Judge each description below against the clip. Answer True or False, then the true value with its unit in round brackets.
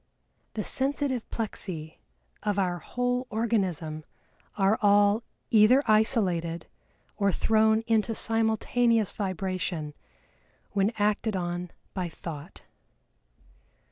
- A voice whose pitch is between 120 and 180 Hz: False (205 Hz)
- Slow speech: True (90 wpm)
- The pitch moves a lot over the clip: False (3.8 semitones)